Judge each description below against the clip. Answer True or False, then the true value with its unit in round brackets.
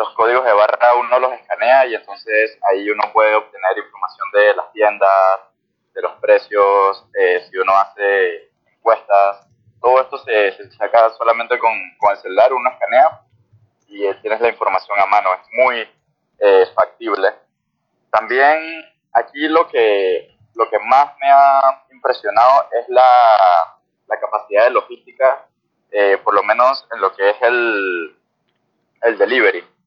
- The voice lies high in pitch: False (125 Hz)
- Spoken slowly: False (150 wpm)